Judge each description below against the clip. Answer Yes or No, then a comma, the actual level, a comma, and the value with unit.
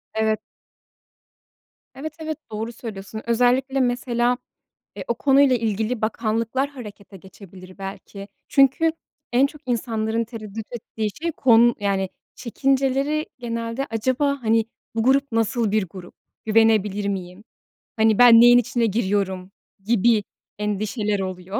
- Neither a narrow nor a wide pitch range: Yes, average, 3.1 semitones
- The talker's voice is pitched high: Yes, high, 225 Hz